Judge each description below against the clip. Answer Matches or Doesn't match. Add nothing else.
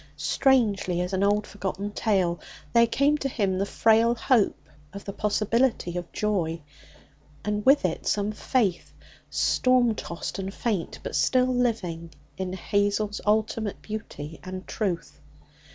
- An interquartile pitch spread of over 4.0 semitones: Doesn't match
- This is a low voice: Doesn't match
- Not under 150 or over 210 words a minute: Doesn't match